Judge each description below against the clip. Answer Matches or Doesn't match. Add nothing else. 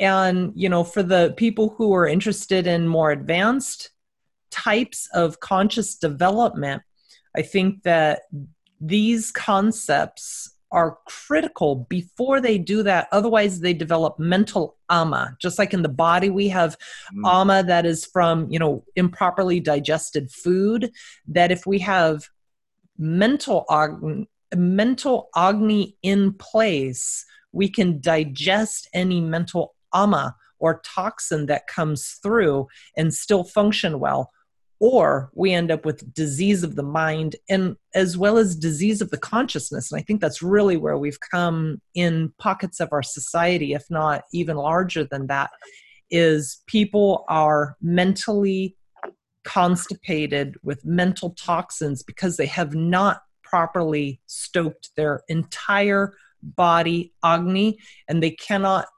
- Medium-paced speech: Doesn't match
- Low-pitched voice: Doesn't match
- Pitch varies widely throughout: Doesn't match